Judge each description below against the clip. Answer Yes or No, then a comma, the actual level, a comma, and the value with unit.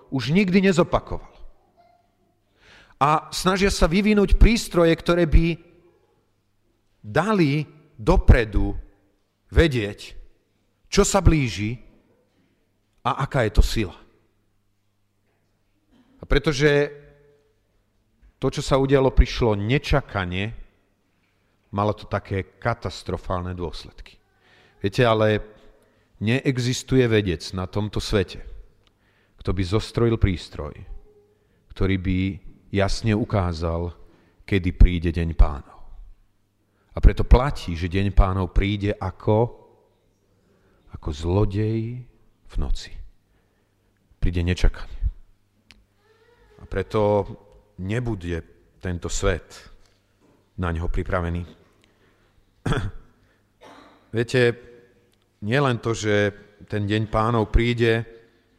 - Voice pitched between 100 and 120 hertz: Yes, low, 105 Hz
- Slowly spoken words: Yes, slow, 85 wpm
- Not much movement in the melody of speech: No, average, 3.7 semitones